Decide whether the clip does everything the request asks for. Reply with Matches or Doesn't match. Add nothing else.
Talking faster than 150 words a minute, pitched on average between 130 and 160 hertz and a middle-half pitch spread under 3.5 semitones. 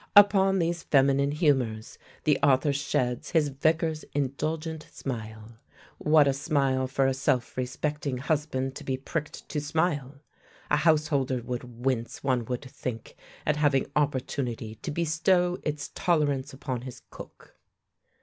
Doesn't match